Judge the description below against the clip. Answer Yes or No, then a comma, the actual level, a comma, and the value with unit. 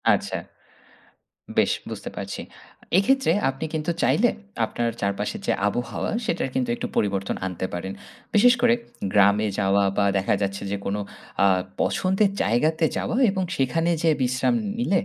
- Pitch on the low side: Yes, low, 125 Hz